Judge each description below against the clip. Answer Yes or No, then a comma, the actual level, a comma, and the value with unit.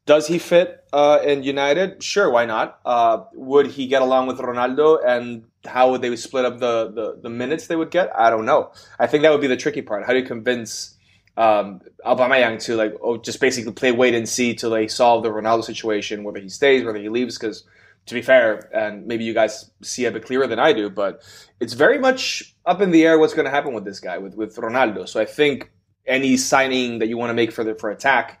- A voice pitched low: Yes, low, 125 Hz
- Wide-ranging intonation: No, average, 3.8 semitones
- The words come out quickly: Yes, fast, 240 wpm